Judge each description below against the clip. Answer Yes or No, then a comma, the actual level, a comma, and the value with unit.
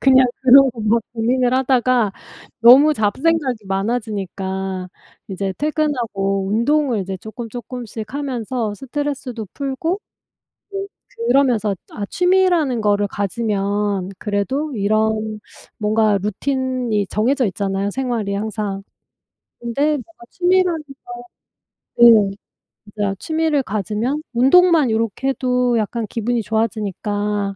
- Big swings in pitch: No, average, 4.5 semitones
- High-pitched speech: Yes, high, 230 Hz